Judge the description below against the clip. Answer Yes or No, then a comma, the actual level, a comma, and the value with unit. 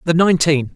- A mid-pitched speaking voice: Yes, medium, 160 Hz